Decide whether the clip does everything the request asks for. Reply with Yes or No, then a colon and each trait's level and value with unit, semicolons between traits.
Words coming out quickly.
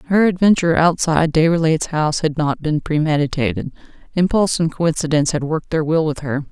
No: average, 165 wpm